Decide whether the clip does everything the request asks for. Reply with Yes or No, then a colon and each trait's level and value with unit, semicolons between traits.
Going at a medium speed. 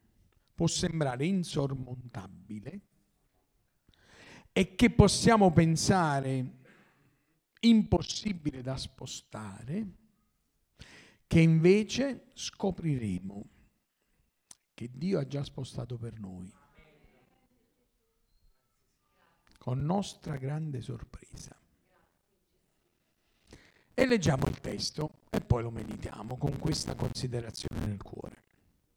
No: slow, 75 wpm